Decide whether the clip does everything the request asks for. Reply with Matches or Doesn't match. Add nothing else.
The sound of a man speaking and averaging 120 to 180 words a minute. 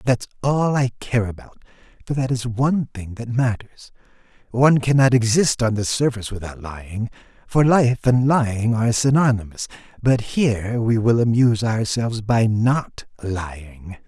Matches